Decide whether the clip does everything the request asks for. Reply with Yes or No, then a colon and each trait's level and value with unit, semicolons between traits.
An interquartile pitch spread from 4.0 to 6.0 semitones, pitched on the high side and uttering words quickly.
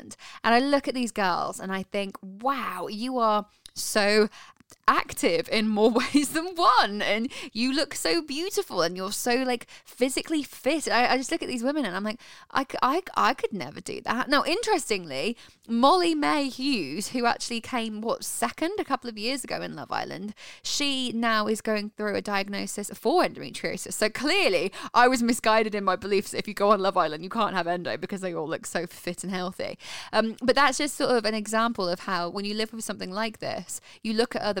Yes: average, 4.8 semitones; high, 225 Hz; fast, 210 wpm